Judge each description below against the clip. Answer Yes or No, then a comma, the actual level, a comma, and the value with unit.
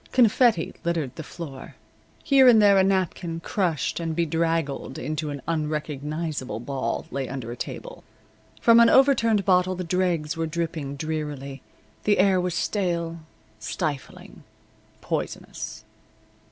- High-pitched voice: No, medium, 165 Hz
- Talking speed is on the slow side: Yes, slow, 125 wpm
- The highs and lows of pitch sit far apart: No, average, 4.0 semitones